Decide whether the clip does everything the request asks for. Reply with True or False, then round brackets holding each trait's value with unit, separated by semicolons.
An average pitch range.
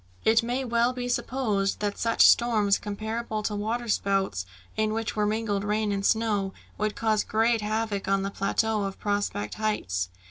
False (2.1 semitones)